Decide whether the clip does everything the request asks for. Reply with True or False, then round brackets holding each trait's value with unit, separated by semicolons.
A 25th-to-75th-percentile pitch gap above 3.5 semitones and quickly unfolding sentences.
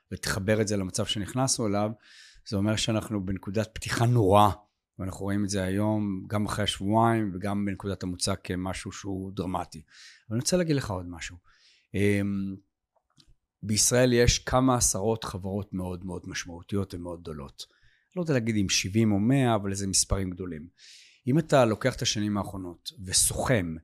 False (3.1 semitones; 155 wpm)